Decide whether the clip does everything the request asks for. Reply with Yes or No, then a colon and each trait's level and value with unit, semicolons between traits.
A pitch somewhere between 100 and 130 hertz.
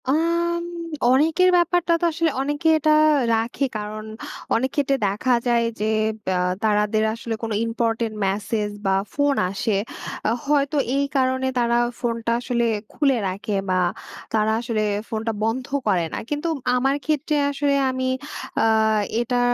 No: high, 245 Hz